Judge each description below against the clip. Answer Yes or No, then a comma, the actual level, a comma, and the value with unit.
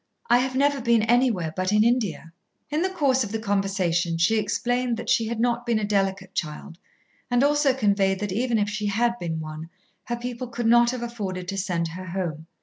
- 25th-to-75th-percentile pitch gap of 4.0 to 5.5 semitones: Yes, average, 4.4 semitones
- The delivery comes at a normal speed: No, fast, 210 wpm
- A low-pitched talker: No, high, 215 Hz